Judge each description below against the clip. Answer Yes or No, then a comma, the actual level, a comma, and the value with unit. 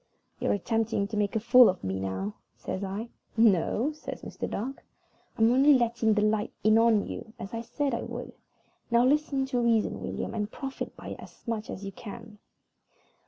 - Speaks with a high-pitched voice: Yes, high, 225 Hz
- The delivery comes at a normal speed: Yes, average, 190 wpm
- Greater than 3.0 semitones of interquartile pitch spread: No, average, 2.7 semitones